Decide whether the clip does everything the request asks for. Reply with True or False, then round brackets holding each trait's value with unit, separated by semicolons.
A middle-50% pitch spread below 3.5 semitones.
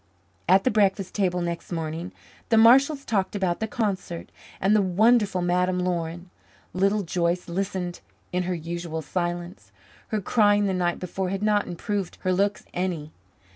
True (2.9 semitones)